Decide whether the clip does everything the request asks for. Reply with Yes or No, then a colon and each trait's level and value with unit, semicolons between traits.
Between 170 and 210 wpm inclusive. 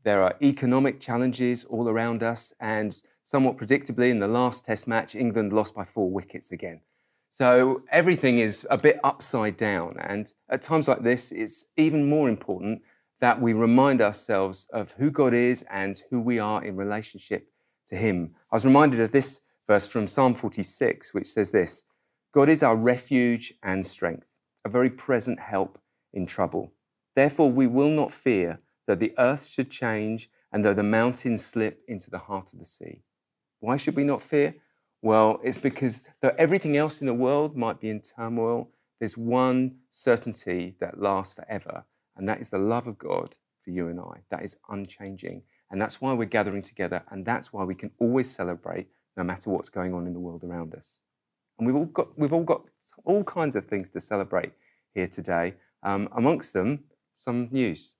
Yes: average, 185 wpm